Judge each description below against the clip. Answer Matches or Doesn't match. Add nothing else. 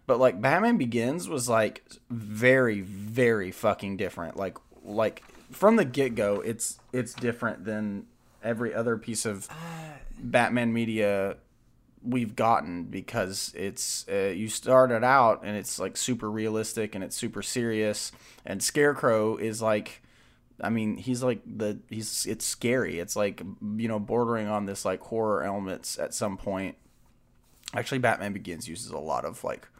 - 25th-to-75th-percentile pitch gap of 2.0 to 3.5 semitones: Matches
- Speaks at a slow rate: Doesn't match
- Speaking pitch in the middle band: Doesn't match